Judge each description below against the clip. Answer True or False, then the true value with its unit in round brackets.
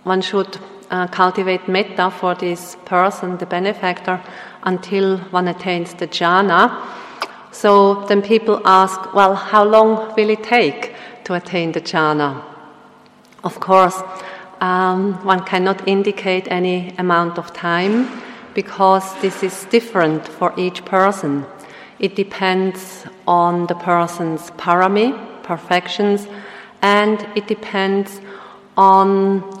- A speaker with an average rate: False (115 wpm)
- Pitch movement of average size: False (1.8 semitones)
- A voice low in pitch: False (190 Hz)